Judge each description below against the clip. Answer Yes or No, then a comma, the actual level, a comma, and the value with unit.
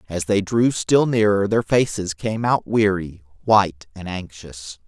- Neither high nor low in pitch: No, low, 100 Hz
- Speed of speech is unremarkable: Yes, average, 160 wpm